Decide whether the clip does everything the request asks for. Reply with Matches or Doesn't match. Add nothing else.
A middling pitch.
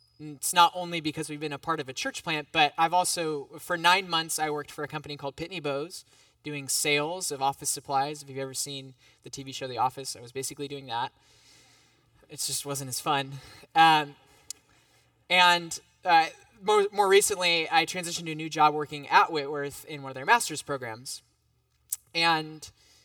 Matches